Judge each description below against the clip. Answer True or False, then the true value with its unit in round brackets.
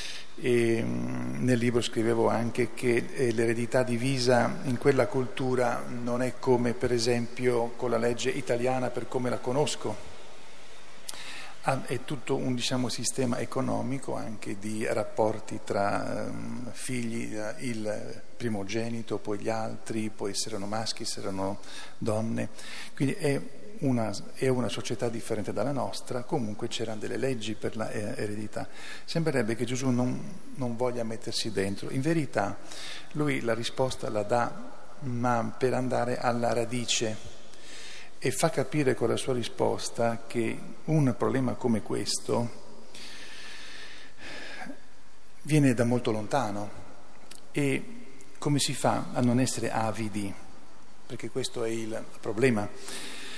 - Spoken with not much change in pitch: True (2.3 semitones)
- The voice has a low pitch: True (120 Hz)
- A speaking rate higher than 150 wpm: False (125 wpm)